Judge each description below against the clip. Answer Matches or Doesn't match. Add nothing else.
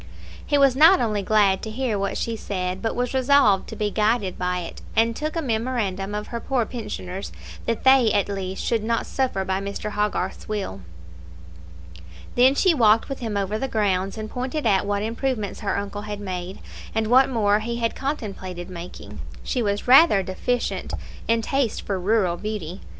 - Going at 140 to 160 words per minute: Doesn't match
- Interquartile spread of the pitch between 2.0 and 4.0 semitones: Matches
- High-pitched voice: Matches